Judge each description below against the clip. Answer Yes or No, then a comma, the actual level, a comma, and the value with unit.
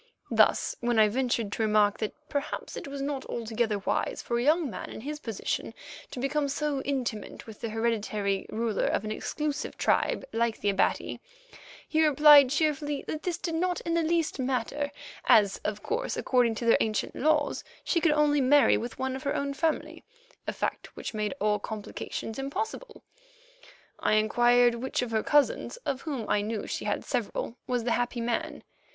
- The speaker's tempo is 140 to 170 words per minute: No, average, 180 wpm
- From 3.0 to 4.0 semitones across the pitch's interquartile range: No, average, 4.9 semitones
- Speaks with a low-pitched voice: No, very high, 255 Hz